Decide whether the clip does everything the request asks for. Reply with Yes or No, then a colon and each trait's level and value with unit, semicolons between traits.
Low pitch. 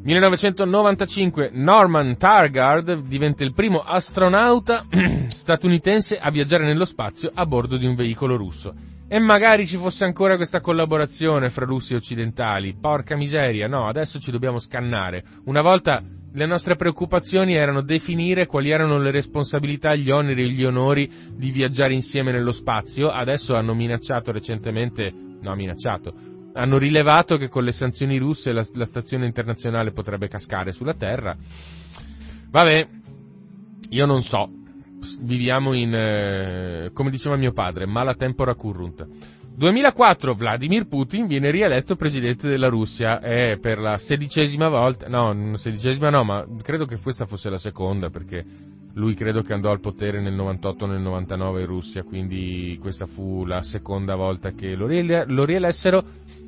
Yes: low, 130 Hz